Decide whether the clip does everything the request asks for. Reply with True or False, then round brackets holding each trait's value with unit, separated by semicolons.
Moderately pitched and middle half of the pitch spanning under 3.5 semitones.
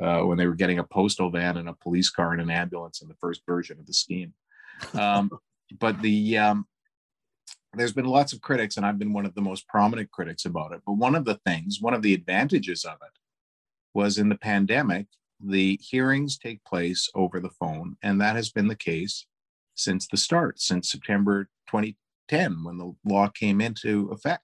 False (100 Hz; 2.9 semitones)